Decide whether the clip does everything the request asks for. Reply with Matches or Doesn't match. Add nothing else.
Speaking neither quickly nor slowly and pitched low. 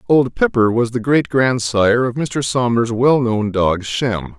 Matches